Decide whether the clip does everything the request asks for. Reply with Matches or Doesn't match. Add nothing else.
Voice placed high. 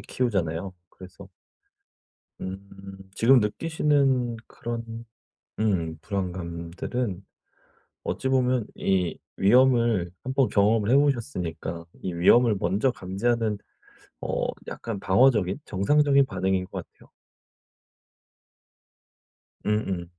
Doesn't match